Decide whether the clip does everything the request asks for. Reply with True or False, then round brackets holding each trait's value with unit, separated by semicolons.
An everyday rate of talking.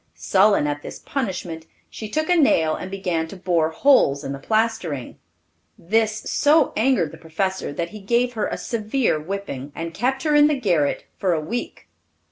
True (180 wpm)